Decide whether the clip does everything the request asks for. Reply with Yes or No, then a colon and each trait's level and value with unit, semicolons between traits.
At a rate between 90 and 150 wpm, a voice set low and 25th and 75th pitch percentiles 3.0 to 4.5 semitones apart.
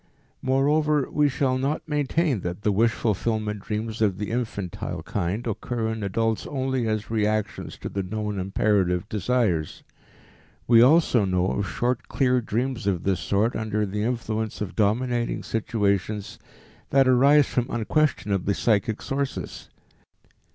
Yes: slow, 135 wpm; low, 110 Hz; average, 3.8 semitones